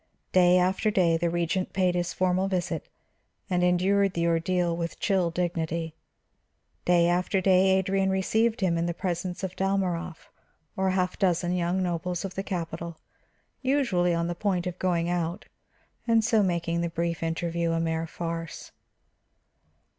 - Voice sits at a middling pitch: Yes, medium, 180 Hz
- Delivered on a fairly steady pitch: Yes, narrow, 2.0 semitones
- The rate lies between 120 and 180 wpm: Yes, average, 155 wpm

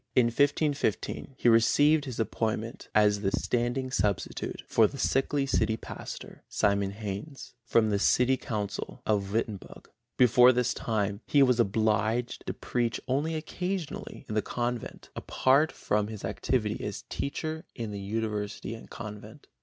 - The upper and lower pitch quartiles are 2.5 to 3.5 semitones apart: No, average, 3.9 semitones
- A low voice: Yes, low, 115 Hz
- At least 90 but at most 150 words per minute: Yes, average, 145 wpm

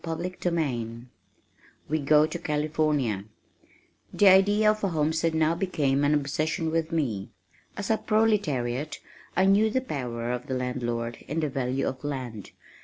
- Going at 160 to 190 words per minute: No, average, 150 wpm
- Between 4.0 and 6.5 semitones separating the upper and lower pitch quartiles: Yes, average, 5.0 semitones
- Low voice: No, medium, 150 Hz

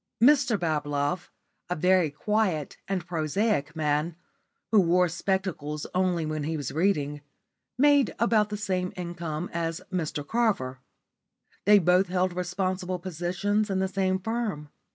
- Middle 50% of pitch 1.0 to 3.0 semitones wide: No, average, 4.0 semitones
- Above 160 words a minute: No, slow, 135 wpm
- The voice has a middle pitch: Yes, medium, 180 Hz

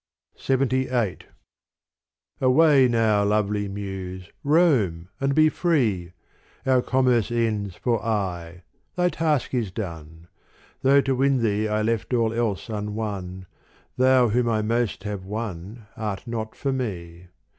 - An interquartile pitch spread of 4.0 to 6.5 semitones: Yes, average, 4.7 semitones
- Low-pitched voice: Yes, low, 110 Hz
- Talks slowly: Yes, slow, 125 wpm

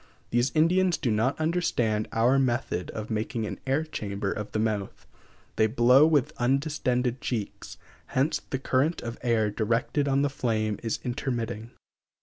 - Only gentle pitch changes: No, average, 3.8 semitones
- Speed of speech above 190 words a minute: No, average, 150 wpm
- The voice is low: Yes, low, 120 Hz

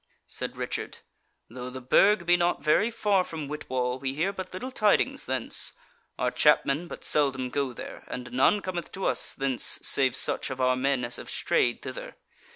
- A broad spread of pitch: Yes, wide, 6.3 semitones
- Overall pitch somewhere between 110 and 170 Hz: Yes, medium, 140 Hz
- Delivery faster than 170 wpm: Yes, average, 180 wpm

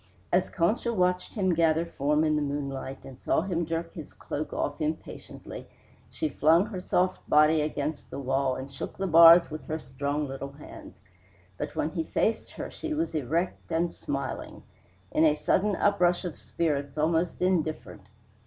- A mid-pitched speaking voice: Yes, medium, 160 Hz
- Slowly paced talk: No, average, 170 wpm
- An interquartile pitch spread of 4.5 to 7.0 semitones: No, average, 3.5 semitones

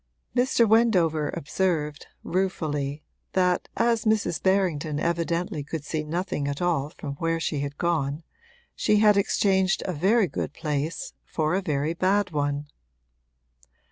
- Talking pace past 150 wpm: No, slow, 135 wpm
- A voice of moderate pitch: Yes, medium, 170 Hz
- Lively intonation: No, average, 4.3 semitones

